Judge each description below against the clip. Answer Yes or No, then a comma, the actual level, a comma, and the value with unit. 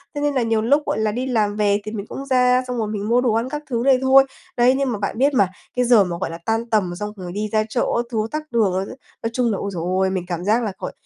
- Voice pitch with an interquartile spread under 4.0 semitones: Yes, average, 3.5 semitones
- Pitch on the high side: Yes, high, 225 Hz